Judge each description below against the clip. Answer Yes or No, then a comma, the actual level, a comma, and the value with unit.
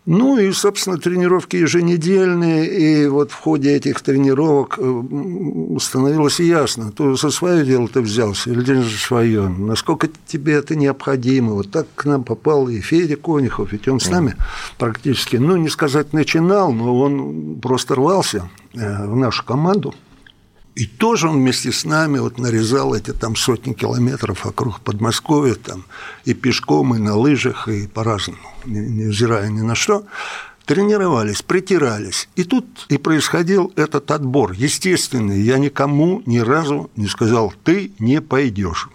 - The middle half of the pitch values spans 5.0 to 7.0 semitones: Yes, wide, 5.6 semitones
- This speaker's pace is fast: No, average, 145 wpm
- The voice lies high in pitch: No, low, 135 Hz